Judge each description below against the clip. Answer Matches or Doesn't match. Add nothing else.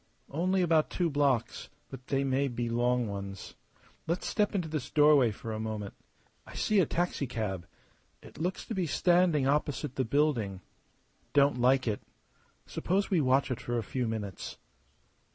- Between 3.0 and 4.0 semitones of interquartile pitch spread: Doesn't match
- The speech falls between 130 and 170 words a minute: Matches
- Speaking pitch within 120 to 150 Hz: Matches